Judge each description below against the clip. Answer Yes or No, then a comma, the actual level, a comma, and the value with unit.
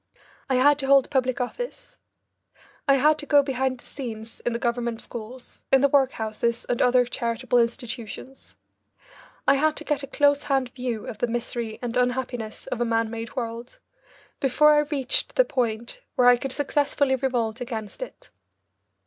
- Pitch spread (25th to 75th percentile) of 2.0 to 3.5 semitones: Yes, average, 2.7 semitones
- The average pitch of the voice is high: Yes, very high, 250 Hz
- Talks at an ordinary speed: Yes, average, 170 wpm